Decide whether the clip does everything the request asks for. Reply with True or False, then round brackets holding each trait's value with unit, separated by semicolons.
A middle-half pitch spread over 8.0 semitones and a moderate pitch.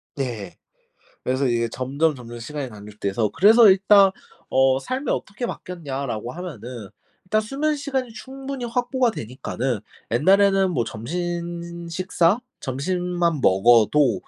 True (8.4 semitones; 165 Hz)